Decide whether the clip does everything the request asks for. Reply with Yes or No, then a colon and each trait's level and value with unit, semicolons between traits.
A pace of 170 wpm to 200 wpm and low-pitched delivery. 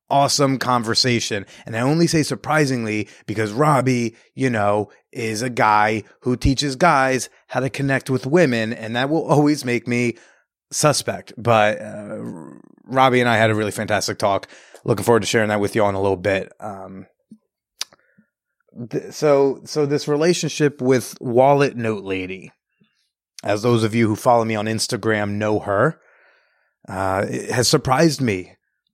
No: average, 160 wpm; low, 120 Hz